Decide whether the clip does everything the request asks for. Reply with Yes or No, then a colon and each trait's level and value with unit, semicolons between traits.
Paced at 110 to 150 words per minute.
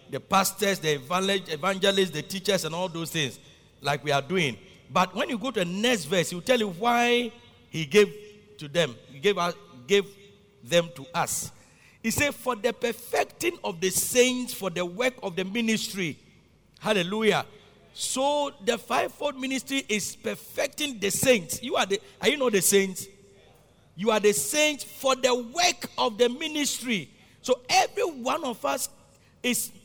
No: average, 170 wpm